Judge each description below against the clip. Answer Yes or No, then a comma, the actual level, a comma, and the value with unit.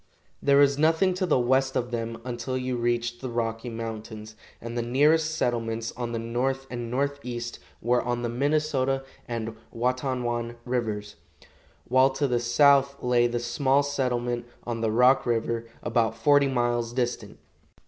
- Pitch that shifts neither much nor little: No, narrow, 2.3 semitones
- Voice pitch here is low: Yes, low, 120 Hz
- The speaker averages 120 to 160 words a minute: Yes, average, 155 wpm